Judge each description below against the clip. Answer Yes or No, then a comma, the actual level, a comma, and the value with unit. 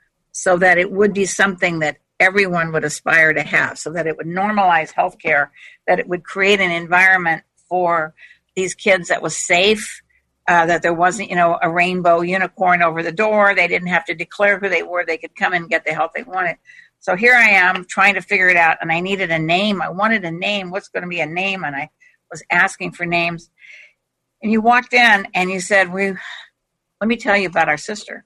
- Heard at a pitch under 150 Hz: No, medium, 180 Hz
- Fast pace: Yes, fast, 220 wpm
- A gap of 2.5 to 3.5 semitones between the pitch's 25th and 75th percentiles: Yes, average, 2.9 semitones